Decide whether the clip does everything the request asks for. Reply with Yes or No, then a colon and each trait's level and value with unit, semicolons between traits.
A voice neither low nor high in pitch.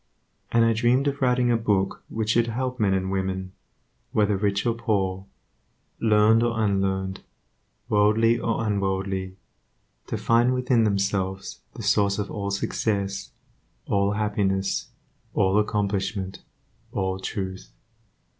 No: low, 105 Hz